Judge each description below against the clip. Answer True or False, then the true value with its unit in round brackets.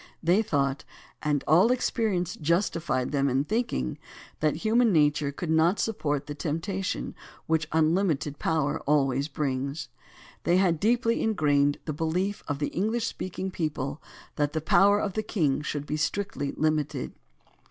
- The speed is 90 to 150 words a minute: True (145 wpm)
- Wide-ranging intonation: False (4.7 semitones)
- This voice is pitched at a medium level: True (155 Hz)